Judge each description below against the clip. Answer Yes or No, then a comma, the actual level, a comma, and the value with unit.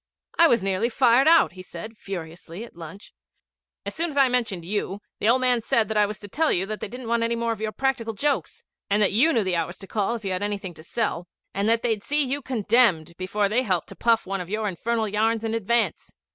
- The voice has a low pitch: No, high, 220 Hz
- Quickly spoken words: Yes, fast, 250 wpm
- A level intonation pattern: No, average, 3.4 semitones